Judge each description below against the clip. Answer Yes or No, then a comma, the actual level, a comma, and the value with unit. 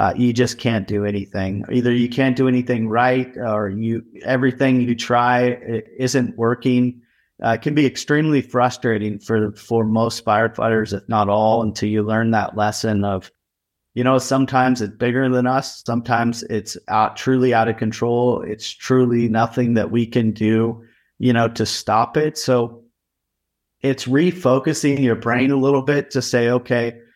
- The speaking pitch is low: Yes, low, 120 Hz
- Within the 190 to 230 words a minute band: No, average, 170 wpm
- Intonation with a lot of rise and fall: No, average, 2.7 semitones